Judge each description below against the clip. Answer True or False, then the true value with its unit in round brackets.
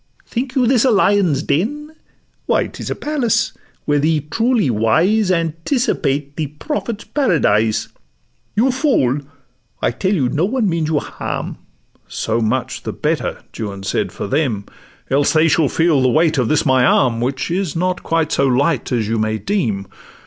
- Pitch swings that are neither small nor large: False (8.0 semitones)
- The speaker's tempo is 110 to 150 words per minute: False (165 wpm)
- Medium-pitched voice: True (155 Hz)